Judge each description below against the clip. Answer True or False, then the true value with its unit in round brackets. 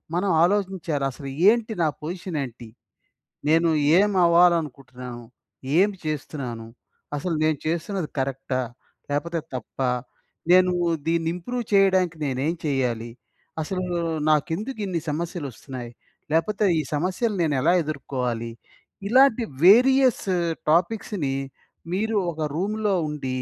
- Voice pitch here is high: False (165 Hz)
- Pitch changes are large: True (5.8 semitones)